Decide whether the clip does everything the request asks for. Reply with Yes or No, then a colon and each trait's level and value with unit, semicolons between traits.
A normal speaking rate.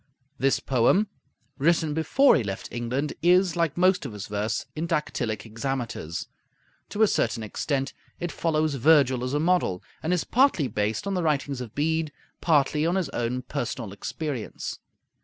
Yes: average, 160 wpm